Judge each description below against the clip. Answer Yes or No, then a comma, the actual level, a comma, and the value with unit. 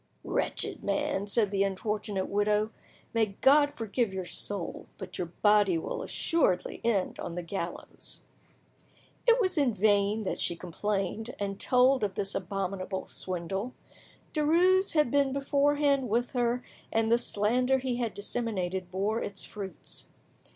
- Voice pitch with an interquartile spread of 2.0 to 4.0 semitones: No, average, 4.5 semitones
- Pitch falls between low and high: No, high, 210 Hz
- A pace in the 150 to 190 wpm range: No, average, 140 wpm